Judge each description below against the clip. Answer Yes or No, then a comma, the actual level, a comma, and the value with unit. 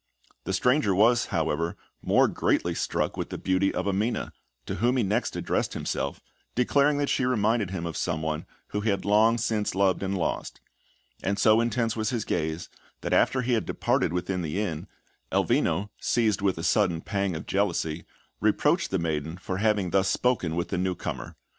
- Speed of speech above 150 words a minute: Yes, average, 180 wpm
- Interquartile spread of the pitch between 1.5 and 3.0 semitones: No, average, 4.5 semitones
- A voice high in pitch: No, low, 100 Hz